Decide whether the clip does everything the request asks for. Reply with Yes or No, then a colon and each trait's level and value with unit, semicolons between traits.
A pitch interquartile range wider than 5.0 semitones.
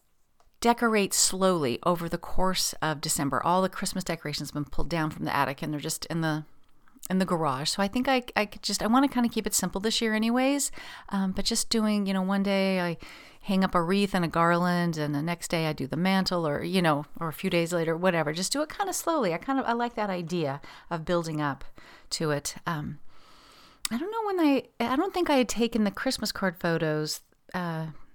Yes: wide, 5.4 semitones